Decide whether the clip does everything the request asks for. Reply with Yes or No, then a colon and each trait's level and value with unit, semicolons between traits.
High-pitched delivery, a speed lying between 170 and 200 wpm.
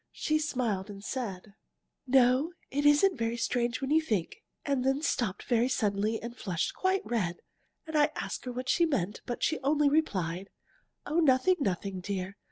Yes: very high, 250 Hz; average, 175 wpm